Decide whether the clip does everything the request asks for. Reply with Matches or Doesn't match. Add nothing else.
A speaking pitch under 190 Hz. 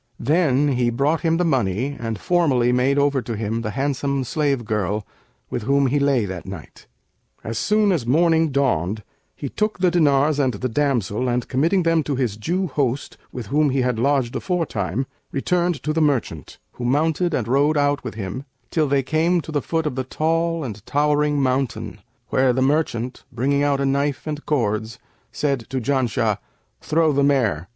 Matches